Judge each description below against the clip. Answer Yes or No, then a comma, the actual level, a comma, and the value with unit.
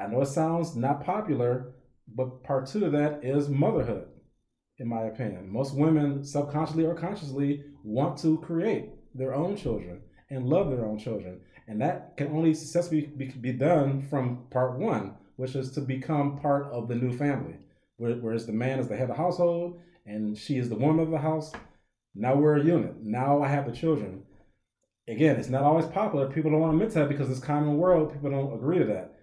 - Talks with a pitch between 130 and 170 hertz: Yes, medium, 140 Hz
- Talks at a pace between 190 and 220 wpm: Yes, average, 200 wpm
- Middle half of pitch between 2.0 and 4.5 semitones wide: Yes, average, 3.9 semitones